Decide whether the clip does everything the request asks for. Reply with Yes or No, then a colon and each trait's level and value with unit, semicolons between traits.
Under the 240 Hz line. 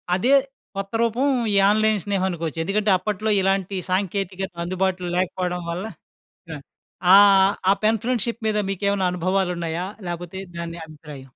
Yes: high, 190 Hz